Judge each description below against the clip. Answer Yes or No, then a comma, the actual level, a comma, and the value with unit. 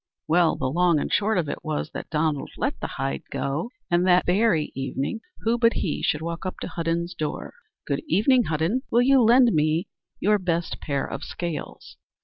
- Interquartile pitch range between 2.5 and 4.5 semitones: No, average, 5.3 semitones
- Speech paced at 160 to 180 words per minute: No, average, 195 wpm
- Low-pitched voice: No, medium, 170 Hz